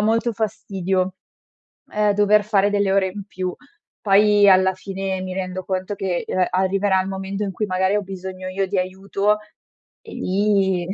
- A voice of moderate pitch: No, high, 195 Hz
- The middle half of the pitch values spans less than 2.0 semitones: Yes, narrow, 1.5 semitones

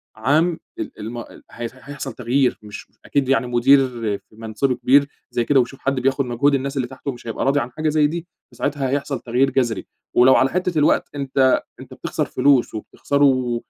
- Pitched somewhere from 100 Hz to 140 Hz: Yes, low, 135 Hz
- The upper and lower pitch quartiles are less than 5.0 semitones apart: Yes, average, 2.7 semitones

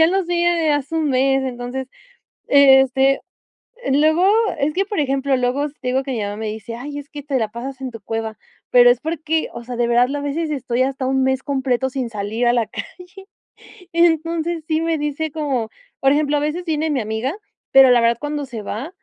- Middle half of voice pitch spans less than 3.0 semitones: No, average, 3.8 semitones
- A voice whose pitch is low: No, very high, 270 Hz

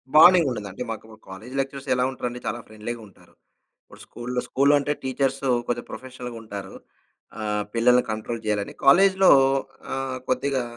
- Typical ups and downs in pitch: Yes, average, 3.2 semitones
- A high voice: No, low, 125 Hz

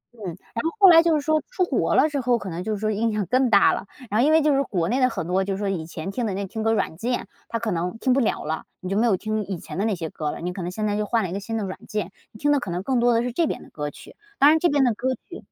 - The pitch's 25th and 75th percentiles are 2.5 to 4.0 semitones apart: No, average, 5.2 semitones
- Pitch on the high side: Yes, high, 215 Hz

